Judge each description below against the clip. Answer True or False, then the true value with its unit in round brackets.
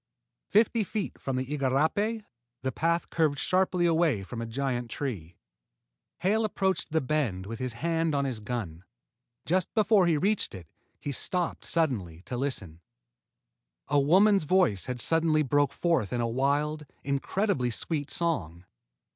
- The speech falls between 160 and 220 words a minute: False (145 wpm)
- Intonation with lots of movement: True (6.0 semitones)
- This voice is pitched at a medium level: True (145 Hz)